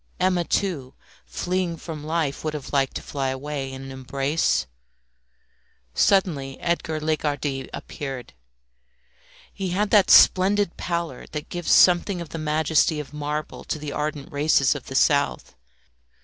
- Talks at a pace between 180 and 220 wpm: No, average, 140 wpm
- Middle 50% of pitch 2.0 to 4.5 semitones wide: Yes, average, 3.8 semitones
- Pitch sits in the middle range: Yes, medium, 150 Hz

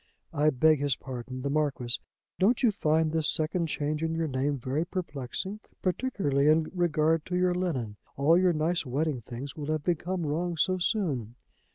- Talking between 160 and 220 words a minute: Yes, average, 175 wpm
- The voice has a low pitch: No, medium, 155 Hz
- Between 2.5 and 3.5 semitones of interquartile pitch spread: No, average, 4.0 semitones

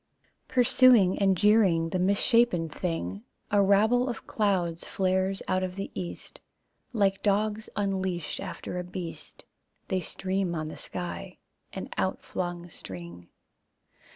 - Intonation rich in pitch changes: No, average, 2.8 semitones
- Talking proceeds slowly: Yes, slow, 125 wpm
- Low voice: No, high, 190 Hz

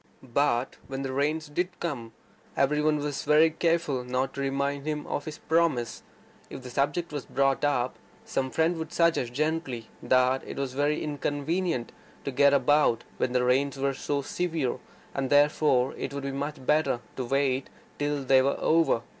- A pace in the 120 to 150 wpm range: No, average, 165 wpm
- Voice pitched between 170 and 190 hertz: No, medium, 140 Hz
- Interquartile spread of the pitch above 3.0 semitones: No, narrow, 2.5 semitones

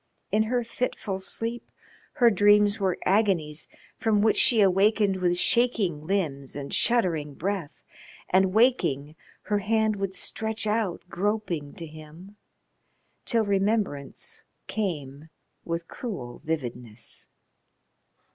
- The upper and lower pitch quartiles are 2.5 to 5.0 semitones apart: No, wide, 5.5 semitones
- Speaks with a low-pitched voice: No, high, 195 Hz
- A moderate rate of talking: No, slow, 110 wpm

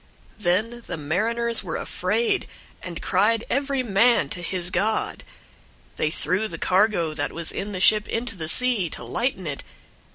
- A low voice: No, high, 205 Hz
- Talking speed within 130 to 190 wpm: Yes, average, 165 wpm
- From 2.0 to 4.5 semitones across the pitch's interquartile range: No, average, 5.0 semitones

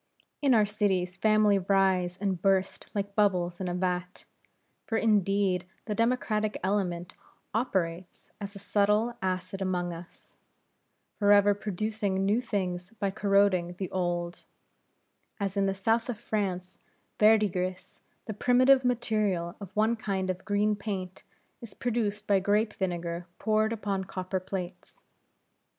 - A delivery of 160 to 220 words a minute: No, slow, 135 wpm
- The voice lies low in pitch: No, high, 195 Hz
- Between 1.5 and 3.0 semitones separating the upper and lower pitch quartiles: Yes, narrow, 2.6 semitones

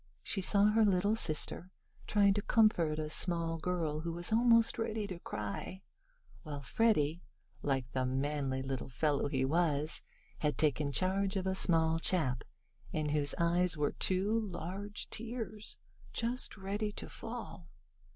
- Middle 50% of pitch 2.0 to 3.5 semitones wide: No, wide, 5.4 semitones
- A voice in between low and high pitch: Yes, medium, 175 Hz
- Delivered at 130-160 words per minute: Yes, average, 145 wpm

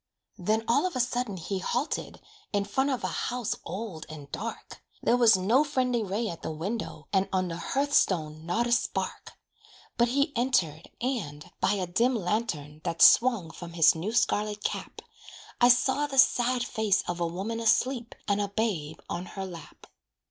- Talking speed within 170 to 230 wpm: Yes, average, 180 wpm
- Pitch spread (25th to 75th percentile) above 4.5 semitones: Yes, wide, 5.6 semitones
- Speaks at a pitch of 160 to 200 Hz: No, high, 210 Hz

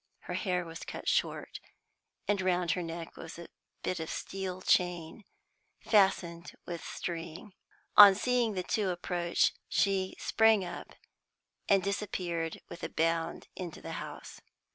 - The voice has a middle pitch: Yes, medium, 180 Hz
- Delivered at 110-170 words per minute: Yes, average, 140 wpm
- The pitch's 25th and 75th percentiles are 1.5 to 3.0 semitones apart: Yes, narrow, 2.6 semitones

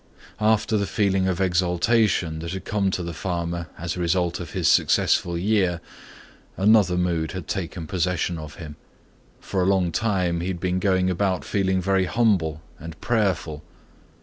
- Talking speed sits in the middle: Yes, average, 165 wpm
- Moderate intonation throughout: No, narrow, 2.3 semitones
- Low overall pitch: Yes, very low, 90 Hz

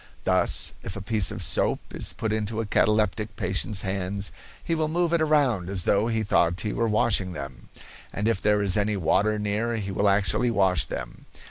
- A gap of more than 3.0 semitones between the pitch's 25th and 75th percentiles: No, average, 2.7 semitones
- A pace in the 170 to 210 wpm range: Yes, average, 200 wpm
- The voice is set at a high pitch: No, low, 105 Hz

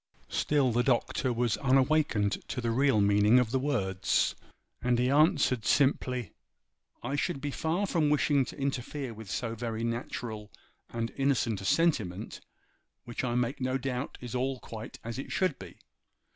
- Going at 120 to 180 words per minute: Yes, average, 160 wpm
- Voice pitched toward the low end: Yes, low, 125 Hz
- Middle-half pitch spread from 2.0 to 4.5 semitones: Yes, average, 3.2 semitones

